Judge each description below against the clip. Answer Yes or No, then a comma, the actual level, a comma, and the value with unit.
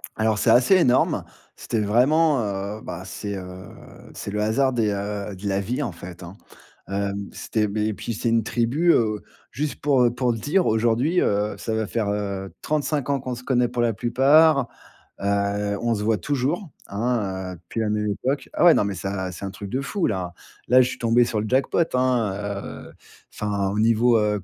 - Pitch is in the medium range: No, low, 110 Hz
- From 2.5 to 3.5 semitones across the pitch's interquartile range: No, average, 3.9 semitones